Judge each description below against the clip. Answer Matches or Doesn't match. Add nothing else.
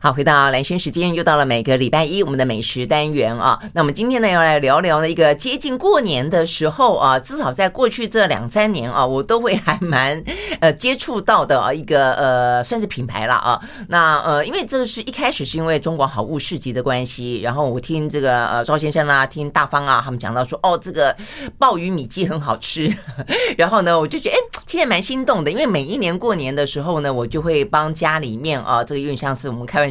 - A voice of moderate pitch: Matches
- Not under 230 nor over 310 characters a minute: Doesn't match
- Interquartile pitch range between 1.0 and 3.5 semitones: Doesn't match